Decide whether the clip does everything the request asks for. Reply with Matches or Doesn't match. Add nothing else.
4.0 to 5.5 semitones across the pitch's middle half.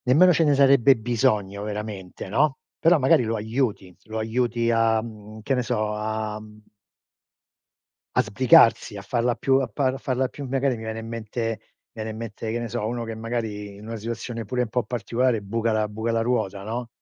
Doesn't match